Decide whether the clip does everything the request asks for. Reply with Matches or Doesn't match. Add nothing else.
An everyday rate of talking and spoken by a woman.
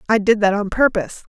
Doesn't match